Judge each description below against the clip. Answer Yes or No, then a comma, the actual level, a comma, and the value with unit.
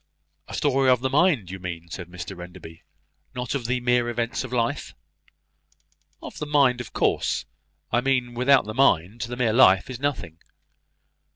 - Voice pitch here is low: Yes, low, 120 Hz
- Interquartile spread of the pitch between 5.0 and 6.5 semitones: Yes, wide, 5.5 semitones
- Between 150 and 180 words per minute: Yes, average, 170 wpm